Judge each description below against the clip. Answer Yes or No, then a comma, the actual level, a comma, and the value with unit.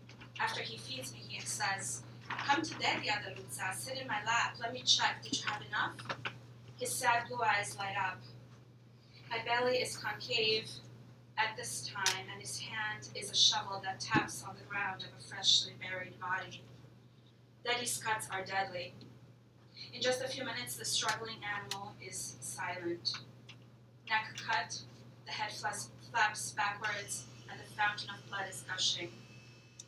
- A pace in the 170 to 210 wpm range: No, average, 155 wpm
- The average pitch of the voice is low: Yes, low, 130 Hz